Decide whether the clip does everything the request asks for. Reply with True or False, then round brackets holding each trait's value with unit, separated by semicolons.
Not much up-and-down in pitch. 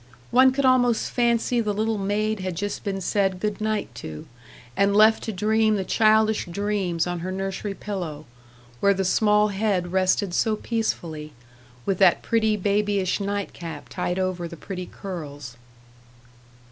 False (3.0 semitones)